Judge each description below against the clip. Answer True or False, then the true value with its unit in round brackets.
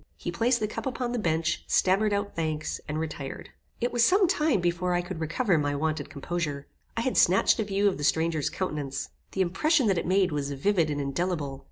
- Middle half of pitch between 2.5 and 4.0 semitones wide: False (5.4 semitones)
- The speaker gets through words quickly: True (210 wpm)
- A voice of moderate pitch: True (175 Hz)